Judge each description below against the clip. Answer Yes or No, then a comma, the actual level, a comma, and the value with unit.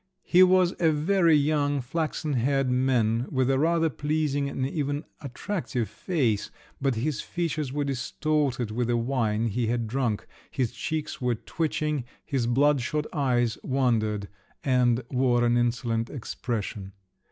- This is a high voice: No, low, 130 Hz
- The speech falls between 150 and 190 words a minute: No, average, 140 wpm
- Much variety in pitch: No, average, 3.9 semitones